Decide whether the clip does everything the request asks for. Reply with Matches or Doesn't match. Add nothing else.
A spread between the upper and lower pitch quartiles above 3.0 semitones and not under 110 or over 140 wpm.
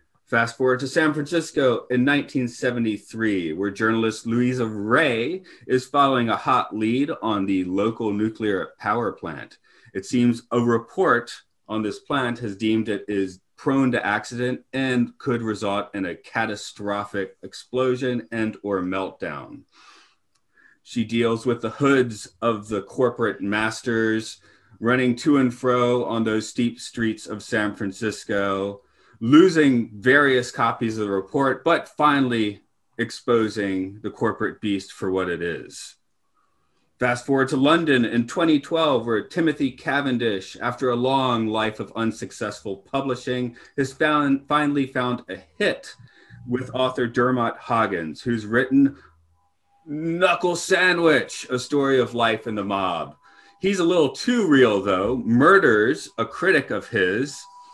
Matches